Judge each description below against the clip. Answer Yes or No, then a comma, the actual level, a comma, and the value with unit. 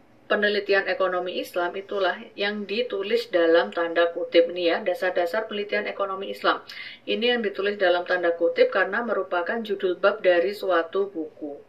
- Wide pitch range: No, average, 2.9 semitones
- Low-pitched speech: No, medium, 185 Hz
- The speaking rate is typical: No, fast, 145 wpm